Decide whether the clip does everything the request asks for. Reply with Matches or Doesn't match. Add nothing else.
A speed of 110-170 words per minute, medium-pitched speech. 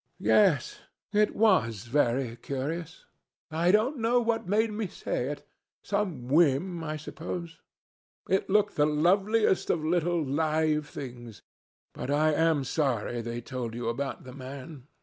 Matches